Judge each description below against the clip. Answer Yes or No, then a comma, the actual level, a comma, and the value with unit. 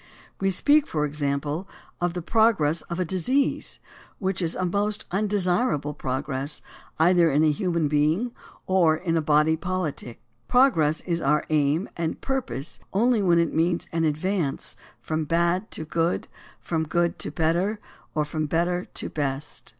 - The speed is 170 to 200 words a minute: No, average, 155 wpm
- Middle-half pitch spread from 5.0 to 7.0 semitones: No, average, 3.6 semitones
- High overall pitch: No, medium, 170 Hz